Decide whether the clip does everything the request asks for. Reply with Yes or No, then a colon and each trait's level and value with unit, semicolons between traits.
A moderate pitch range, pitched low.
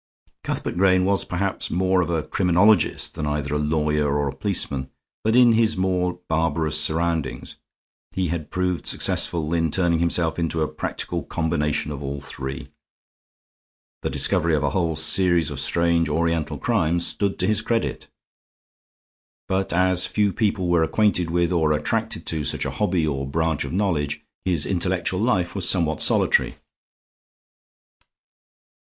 Yes: average, 3.3 semitones; very low, 85 Hz